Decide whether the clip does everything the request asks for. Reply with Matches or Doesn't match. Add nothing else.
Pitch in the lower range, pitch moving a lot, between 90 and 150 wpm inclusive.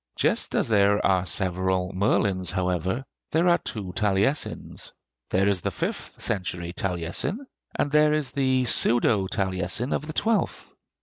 Matches